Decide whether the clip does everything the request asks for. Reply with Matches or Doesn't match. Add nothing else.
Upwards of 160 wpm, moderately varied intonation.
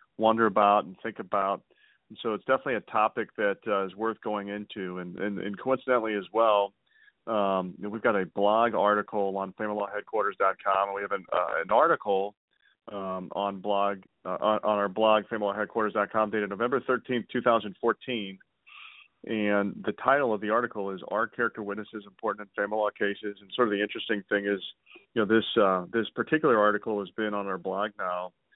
Doesn't match